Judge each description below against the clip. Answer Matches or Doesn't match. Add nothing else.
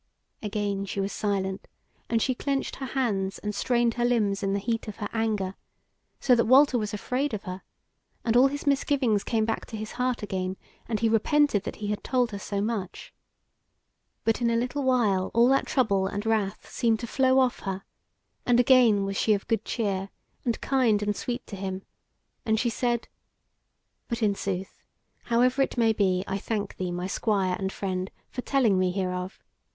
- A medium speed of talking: Matches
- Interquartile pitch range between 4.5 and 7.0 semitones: Doesn't match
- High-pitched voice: Matches